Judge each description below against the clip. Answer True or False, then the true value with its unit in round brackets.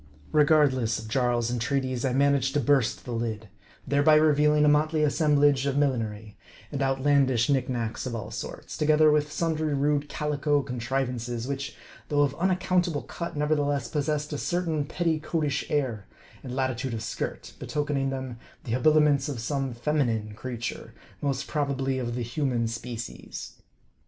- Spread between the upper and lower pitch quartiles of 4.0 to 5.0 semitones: False (3.4 semitones)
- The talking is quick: False (150 wpm)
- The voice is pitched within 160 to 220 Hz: False (140 Hz)